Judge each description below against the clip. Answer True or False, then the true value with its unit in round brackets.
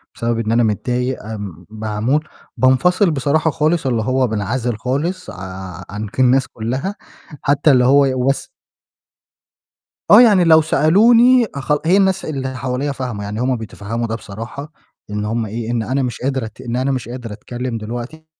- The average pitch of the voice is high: False (125 Hz)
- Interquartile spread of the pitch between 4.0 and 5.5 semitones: True (4.5 semitones)